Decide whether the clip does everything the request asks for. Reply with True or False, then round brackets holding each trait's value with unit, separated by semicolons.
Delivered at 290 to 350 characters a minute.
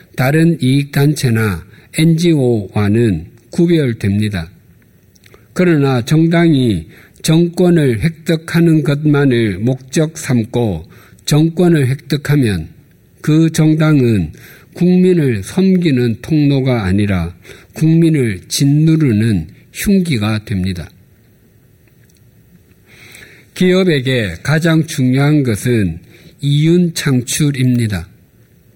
False (190 characters per minute)